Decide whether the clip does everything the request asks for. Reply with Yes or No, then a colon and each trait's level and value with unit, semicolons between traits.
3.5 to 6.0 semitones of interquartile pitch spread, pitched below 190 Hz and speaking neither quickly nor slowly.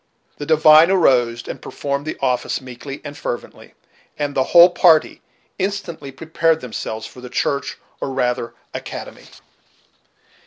No: average, 4.2 semitones; medium, 140 Hz; slow, 130 wpm